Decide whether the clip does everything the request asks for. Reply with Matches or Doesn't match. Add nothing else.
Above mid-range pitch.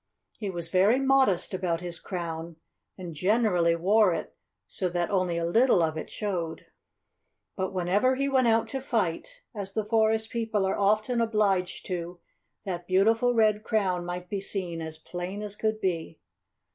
Matches